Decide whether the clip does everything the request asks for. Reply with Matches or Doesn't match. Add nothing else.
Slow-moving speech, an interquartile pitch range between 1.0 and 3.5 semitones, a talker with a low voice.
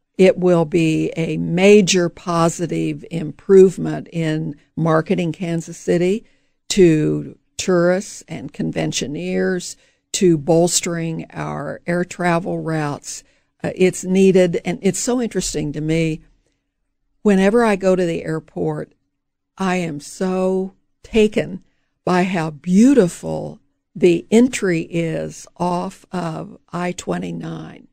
Doesn't match